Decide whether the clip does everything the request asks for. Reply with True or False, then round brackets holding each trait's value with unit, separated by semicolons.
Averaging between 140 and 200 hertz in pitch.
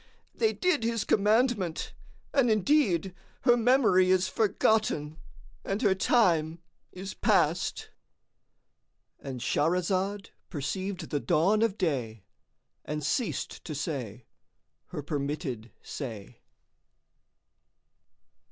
True (185 Hz)